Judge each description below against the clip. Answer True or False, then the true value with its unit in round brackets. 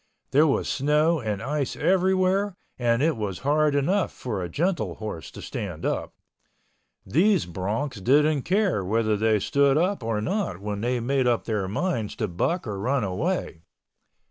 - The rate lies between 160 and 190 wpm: True (165 wpm)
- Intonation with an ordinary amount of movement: False (7.4 semitones)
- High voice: False (130 Hz)